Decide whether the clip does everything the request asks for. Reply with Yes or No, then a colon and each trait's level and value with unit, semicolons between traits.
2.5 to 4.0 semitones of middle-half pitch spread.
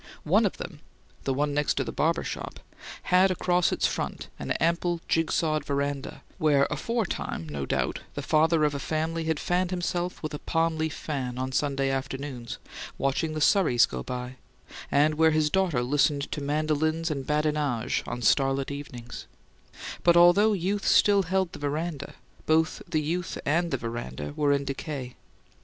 Yes: average, 3.3 semitones